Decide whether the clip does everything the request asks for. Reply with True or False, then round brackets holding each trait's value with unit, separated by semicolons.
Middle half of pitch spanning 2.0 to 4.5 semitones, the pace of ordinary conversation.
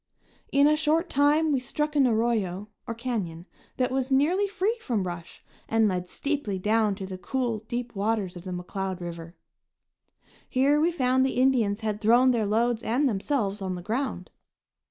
False (5.6 semitones; 175 wpm)